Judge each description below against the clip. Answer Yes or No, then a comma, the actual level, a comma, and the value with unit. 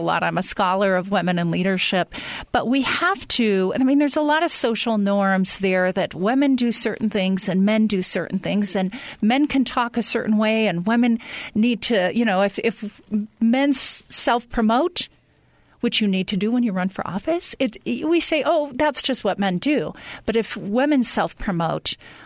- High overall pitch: Yes, high, 220 Hz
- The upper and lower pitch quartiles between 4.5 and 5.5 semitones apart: Yes, average, 5.1 semitones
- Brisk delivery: No, average, 190 wpm